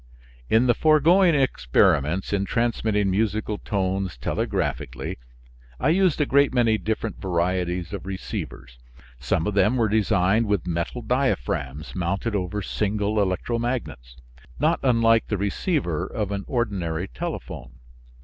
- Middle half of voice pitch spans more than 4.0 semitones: Yes, average, 4.7 semitones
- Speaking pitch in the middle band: No, low, 105 Hz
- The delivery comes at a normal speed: No, slow, 125 wpm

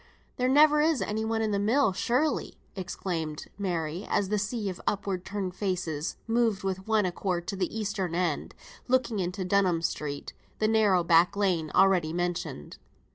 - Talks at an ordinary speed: Yes, average, 160 wpm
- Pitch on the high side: Yes, high, 195 Hz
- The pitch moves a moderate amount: Yes, average, 3.7 semitones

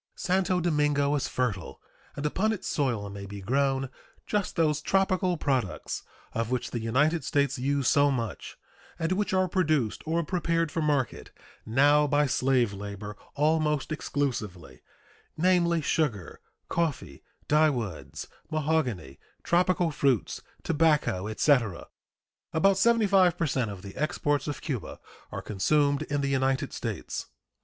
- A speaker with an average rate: No, slow, 130 wpm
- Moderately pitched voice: Yes, medium, 145 Hz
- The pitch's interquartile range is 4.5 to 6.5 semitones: Yes, average, 5.2 semitones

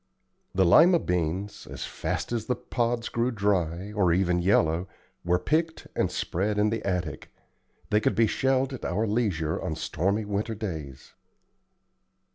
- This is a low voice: Yes, low, 100 Hz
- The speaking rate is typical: Yes, average, 150 wpm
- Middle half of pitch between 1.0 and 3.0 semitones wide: No, average, 4.7 semitones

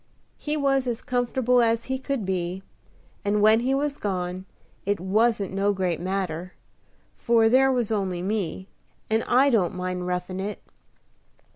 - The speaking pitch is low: No, high, 205 Hz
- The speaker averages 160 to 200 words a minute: No, average, 150 wpm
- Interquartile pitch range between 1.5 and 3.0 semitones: No, average, 4.8 semitones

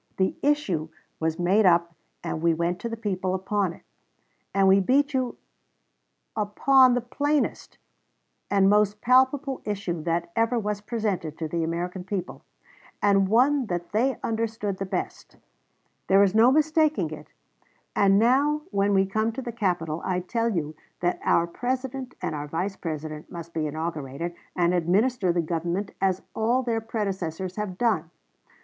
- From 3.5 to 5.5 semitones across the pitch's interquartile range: Yes, average, 5.1 semitones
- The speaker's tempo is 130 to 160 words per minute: Yes, average, 155 wpm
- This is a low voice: No, high, 195 Hz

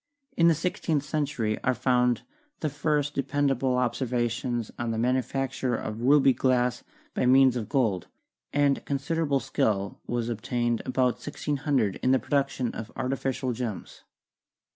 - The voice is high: No, low, 130 Hz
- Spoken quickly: No, average, 140 wpm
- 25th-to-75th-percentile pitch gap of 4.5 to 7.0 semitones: No, average, 2.7 semitones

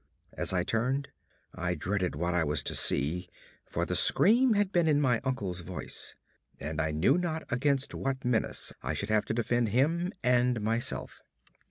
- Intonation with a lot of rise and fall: Yes, wide, 7.8 semitones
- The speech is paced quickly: No, average, 175 wpm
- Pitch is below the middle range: Yes, low, 120 Hz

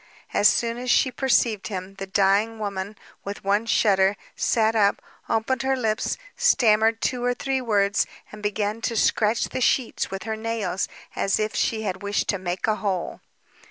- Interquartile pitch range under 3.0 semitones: Yes, narrow, 2.4 semitones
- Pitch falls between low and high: No, high, 215 Hz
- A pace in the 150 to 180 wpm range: Yes, average, 175 wpm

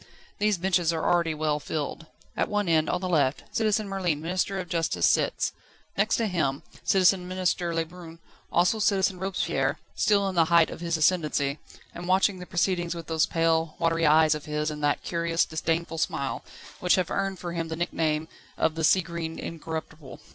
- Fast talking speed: No, average, 185 wpm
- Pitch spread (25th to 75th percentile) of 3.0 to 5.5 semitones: No, narrow, 2.5 semitones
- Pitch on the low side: No, medium, 170 Hz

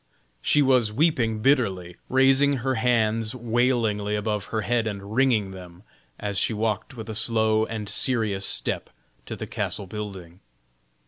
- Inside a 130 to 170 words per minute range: Yes, average, 145 wpm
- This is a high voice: No, low, 110 Hz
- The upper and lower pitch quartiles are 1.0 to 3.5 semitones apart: Yes, average, 3.0 semitones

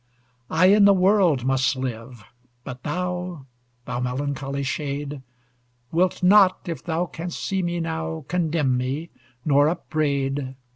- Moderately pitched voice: Yes, medium, 155 Hz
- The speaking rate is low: Yes, slow, 130 wpm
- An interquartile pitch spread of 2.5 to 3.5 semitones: No, average, 4.8 semitones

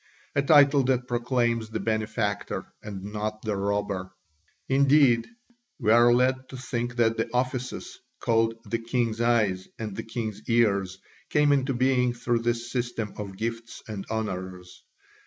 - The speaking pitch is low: Yes, low, 115 Hz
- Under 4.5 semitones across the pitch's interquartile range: Yes, average, 2.8 semitones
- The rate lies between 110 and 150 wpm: Yes, average, 145 wpm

